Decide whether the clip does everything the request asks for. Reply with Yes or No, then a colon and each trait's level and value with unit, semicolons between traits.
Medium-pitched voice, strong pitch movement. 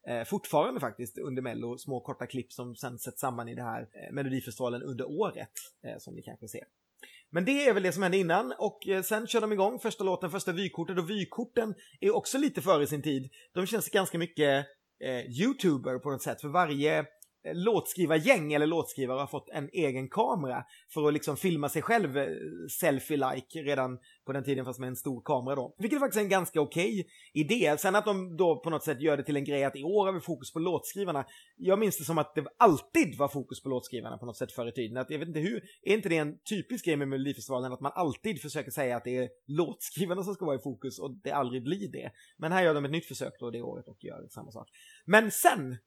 Yes: medium, 150 Hz; wide, 6.2 semitones